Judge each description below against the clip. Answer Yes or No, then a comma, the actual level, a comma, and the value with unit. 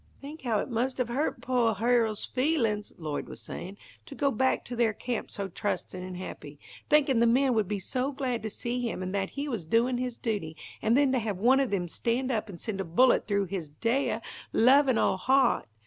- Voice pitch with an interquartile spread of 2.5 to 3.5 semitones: No, average, 4.4 semitones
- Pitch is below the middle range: No, high, 230 Hz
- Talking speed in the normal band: No, fast, 220 wpm